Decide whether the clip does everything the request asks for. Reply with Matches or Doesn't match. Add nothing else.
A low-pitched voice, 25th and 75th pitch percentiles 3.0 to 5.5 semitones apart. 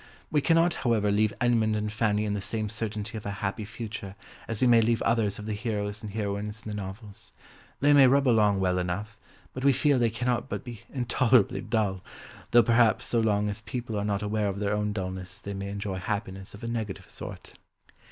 Doesn't match